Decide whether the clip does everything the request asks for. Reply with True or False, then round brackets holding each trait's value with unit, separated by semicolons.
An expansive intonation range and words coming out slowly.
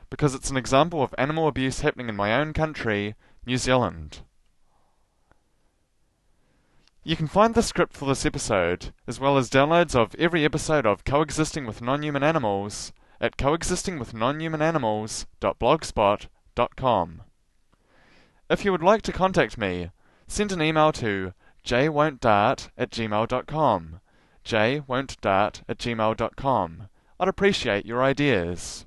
True (6.4 semitones; 120 wpm)